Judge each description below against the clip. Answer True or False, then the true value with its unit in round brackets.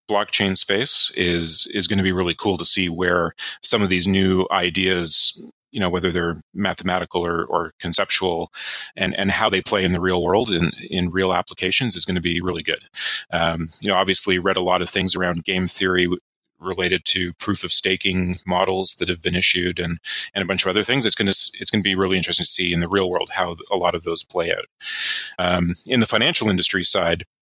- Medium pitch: False (95 Hz)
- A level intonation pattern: True (1.7 semitones)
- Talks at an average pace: False (220 wpm)